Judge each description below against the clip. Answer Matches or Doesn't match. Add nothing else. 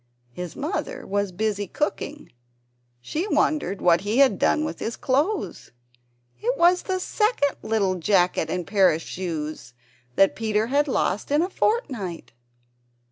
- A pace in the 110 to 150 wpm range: Matches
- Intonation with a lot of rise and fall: Matches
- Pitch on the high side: Matches